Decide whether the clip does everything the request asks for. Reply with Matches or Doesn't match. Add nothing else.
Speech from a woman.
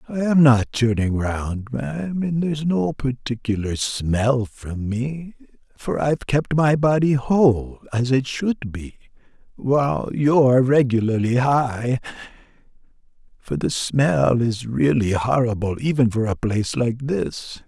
Doesn't match